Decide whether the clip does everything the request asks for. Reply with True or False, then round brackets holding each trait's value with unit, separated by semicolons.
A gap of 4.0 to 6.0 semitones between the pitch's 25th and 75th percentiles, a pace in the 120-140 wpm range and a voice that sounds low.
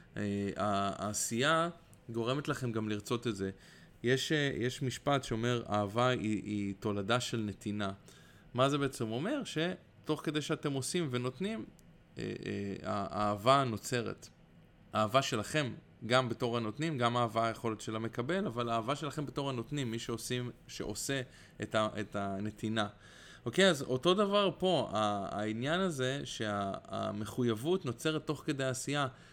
True (5.0 semitones; 135 wpm; 120 Hz)